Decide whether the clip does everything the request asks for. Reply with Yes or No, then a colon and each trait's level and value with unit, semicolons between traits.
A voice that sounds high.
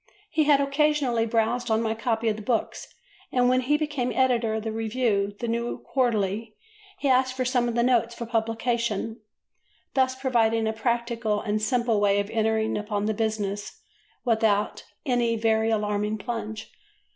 Yes: high, 230 Hz